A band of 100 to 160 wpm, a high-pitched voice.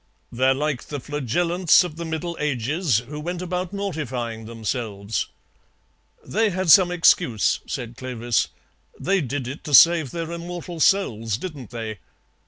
No: average, 140 wpm; medium, 150 Hz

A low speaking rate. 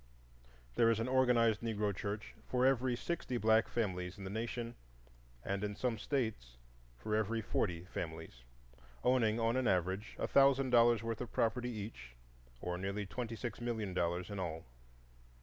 No: average, 160 wpm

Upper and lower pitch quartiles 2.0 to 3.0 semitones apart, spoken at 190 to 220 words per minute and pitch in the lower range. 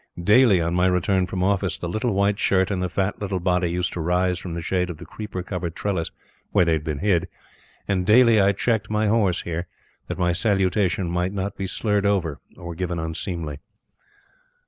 Yes: narrow, 2.5 semitones; average, 200 wpm; very low, 90 Hz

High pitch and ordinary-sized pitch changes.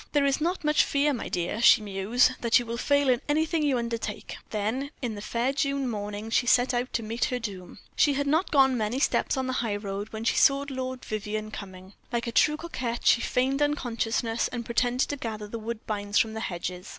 Yes: high, 235 Hz; average, 4.1 semitones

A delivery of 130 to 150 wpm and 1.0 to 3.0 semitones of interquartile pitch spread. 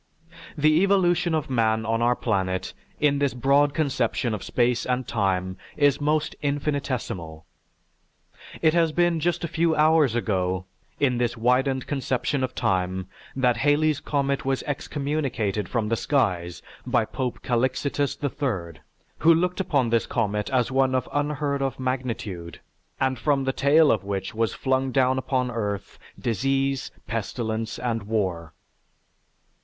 No: average, 145 wpm; average, 4.4 semitones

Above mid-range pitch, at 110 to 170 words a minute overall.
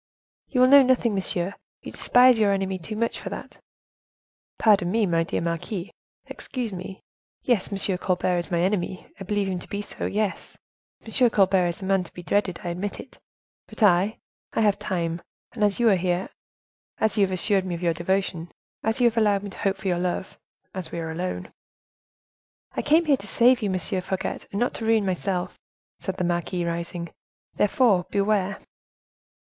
No: high, 195 Hz; average, 190 wpm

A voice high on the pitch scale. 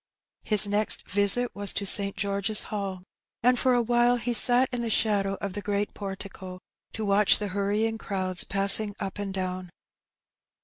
Yes: high, 205 Hz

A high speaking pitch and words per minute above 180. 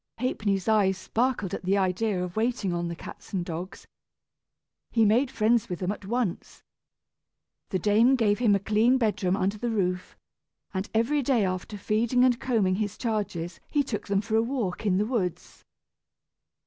No: high, 210 Hz; average, 175 wpm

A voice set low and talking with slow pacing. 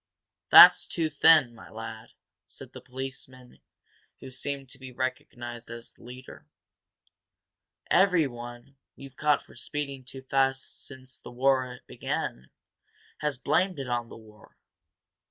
Yes: low, 130 Hz; slow, 130 wpm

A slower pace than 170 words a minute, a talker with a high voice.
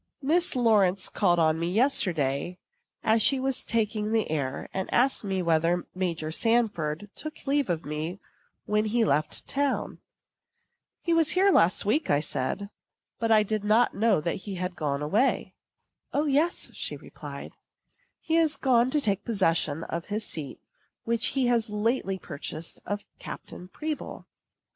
Yes: average, 155 wpm; high, 210 Hz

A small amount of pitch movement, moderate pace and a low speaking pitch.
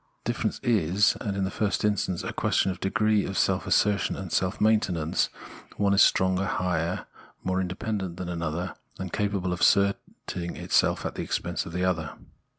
Yes: narrow, 2.3 semitones; average, 170 wpm; very low, 95 Hz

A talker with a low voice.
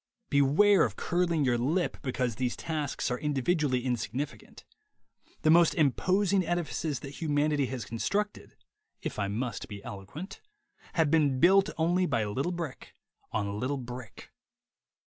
No: medium, 145 Hz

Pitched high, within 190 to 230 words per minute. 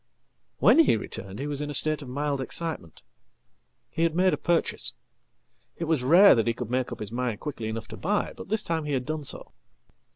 No: medium, 145 Hz; fast, 205 wpm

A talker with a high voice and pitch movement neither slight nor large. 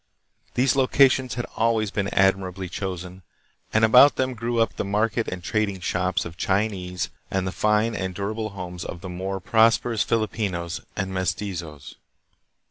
No: low, 100 Hz; average, 3.5 semitones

